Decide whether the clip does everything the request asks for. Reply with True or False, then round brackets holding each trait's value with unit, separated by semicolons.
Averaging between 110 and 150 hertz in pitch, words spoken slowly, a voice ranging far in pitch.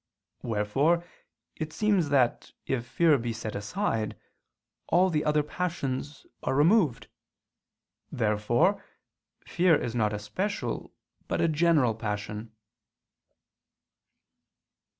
True (140 Hz; 100 wpm; 7.3 semitones)